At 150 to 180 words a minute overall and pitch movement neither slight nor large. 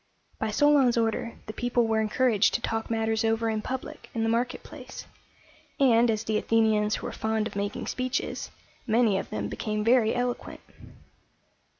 No: average, 165 wpm; narrow, 2.0 semitones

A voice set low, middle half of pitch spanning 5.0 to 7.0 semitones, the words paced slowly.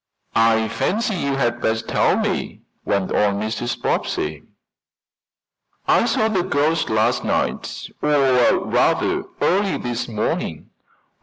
Yes: low, 120 Hz; wide, 5.4 semitones; slow, 120 wpm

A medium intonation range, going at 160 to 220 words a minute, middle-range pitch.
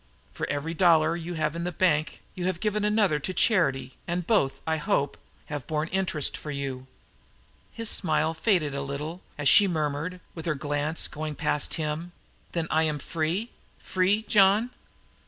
Yes: average, 3.5 semitones; average, 170 wpm; medium, 160 Hz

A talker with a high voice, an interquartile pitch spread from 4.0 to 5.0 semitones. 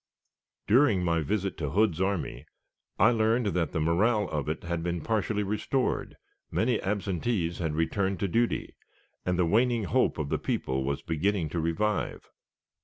No: very low, 95 Hz; average, 4.6 semitones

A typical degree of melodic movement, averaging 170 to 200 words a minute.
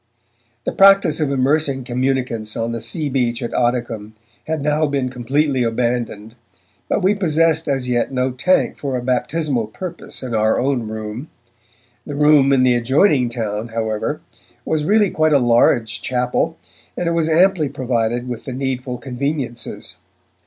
No: average, 4.0 semitones; average, 155 wpm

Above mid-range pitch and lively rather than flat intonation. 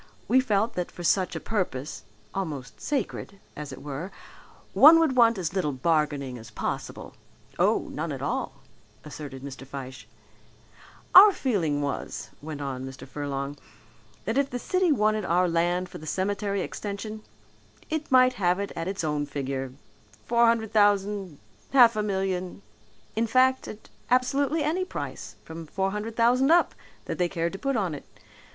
Yes: high, 195 Hz; wide, 7.6 semitones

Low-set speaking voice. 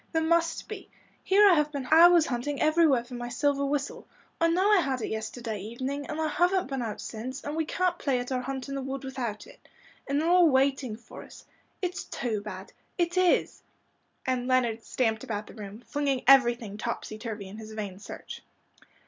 No: very high, 265 Hz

